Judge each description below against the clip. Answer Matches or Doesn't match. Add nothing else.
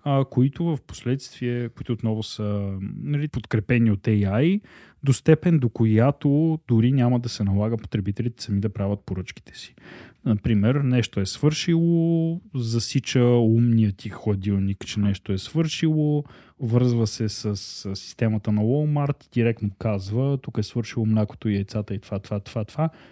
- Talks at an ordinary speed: Matches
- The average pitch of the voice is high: Doesn't match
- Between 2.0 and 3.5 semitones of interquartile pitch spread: Doesn't match